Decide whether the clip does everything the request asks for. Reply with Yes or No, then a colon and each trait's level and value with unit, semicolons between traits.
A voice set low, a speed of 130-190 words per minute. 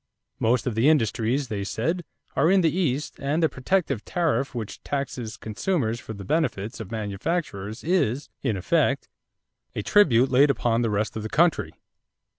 Yes: low, 125 Hz; average, 165 wpm